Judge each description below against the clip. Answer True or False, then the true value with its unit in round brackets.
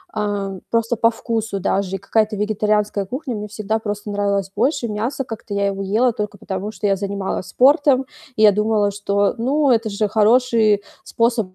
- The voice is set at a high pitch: True (210 Hz)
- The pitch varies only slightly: True (2.2 semitones)